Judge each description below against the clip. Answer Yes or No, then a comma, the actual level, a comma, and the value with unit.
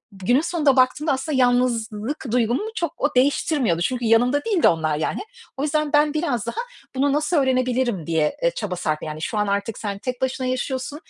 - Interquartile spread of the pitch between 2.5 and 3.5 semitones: No, wide, 5.4 semitones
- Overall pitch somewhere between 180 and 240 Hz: No, very high, 255 Hz